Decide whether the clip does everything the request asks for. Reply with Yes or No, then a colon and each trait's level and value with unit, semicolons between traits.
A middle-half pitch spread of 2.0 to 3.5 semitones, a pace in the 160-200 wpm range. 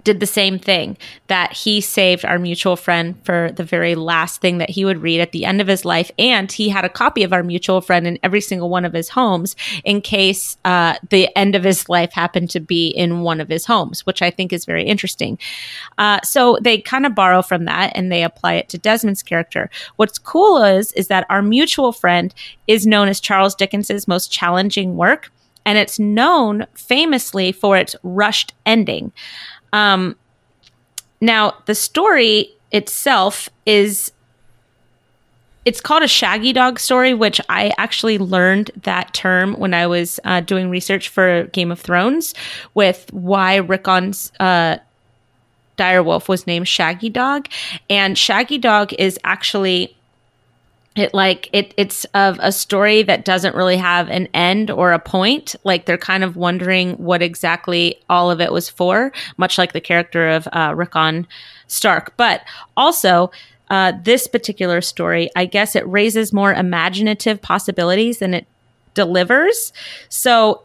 Yes: average, 3.1 semitones; average, 170 wpm